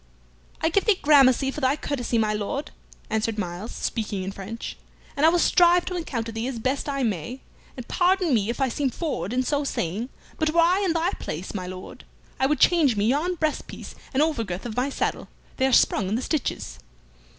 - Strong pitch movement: Yes, wide, 6.0 semitones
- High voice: Yes, very high, 260 Hz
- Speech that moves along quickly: Yes, fast, 215 wpm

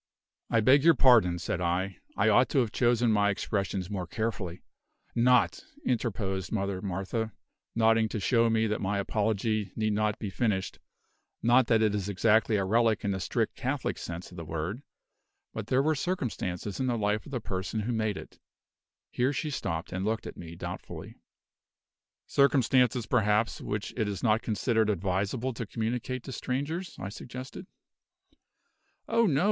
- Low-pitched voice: Yes, low, 110 Hz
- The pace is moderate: Yes, average, 170 wpm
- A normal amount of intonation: Yes, average, 3.7 semitones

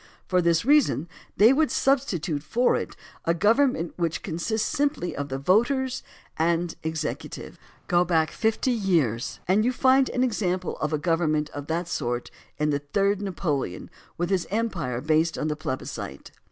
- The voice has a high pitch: No, medium, 175 Hz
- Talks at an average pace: Yes, average, 160 wpm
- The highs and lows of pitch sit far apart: Yes, wide, 6.2 semitones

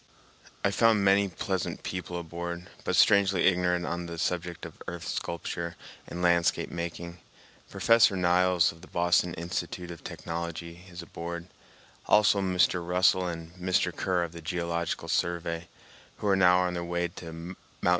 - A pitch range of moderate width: No, narrow, 1.1 semitones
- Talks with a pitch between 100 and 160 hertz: No, very low, 85 Hz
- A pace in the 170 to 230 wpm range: No, average, 155 wpm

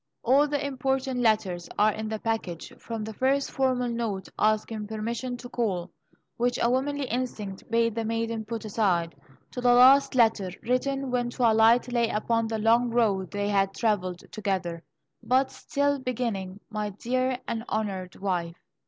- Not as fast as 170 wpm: Yes, average, 160 wpm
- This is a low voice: No, high, 230 Hz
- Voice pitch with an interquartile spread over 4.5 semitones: No, average, 3.2 semitones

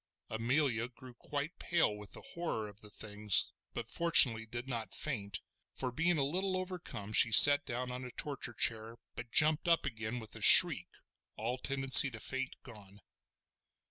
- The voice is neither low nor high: No, low, 125 Hz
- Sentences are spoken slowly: No, average, 170 wpm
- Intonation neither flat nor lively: Yes, average, 4.6 semitones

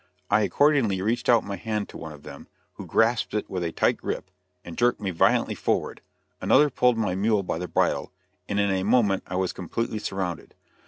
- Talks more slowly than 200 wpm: No, fast, 205 wpm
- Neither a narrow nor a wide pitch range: Yes, average, 3.6 semitones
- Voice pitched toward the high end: No, low, 100 Hz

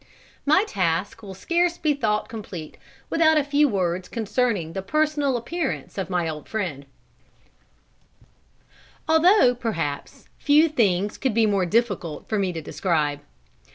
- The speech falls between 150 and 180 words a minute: No, slow, 135 wpm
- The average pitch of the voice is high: Yes, high, 215 Hz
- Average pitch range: No, wide, 8.2 semitones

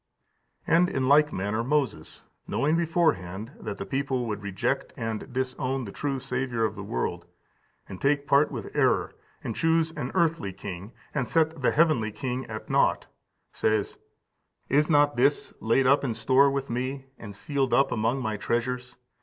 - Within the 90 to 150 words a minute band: No, average, 165 wpm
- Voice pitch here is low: Yes, low, 130 Hz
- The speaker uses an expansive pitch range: No, average, 4.4 semitones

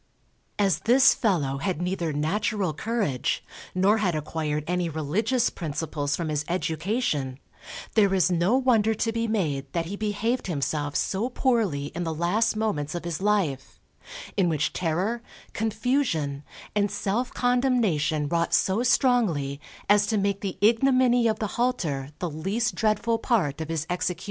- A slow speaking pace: No, average, 150 wpm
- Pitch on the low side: No, high, 190 Hz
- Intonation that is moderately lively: No, wide, 6.2 semitones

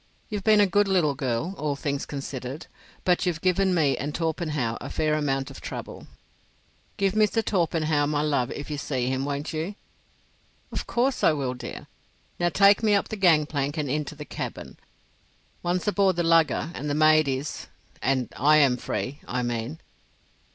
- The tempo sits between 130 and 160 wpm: No, average, 175 wpm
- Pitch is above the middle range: No, medium, 155 Hz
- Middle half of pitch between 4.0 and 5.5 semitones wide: Yes, average, 4.4 semitones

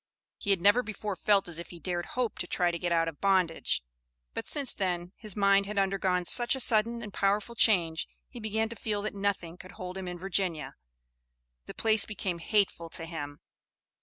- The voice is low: No, high, 195 Hz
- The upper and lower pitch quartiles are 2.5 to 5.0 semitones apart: Yes, average, 3.4 semitones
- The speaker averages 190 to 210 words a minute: Yes, average, 200 wpm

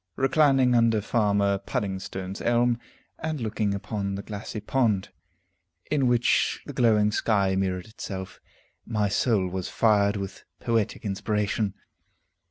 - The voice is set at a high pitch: No, low, 105 Hz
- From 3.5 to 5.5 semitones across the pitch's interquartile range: No, average, 3.0 semitones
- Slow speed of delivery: Yes, slow, 120 wpm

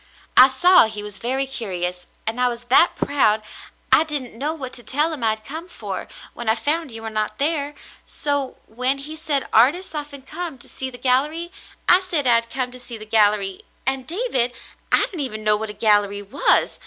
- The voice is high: Yes, very high, 255 Hz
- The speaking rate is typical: No, fast, 210 wpm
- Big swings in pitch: No, average, 5.0 semitones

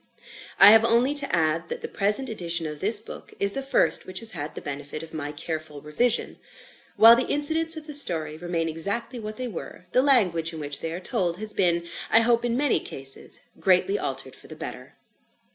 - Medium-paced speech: No, fast, 210 wpm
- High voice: Yes, high, 195 Hz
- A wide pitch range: Yes, wide, 6.5 semitones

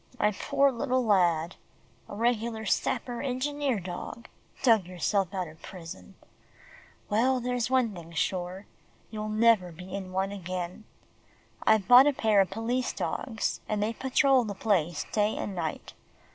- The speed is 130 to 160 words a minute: Yes, average, 145 wpm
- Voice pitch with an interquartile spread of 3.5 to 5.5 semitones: Yes, average, 4.8 semitones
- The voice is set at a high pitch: Yes, high, 210 Hz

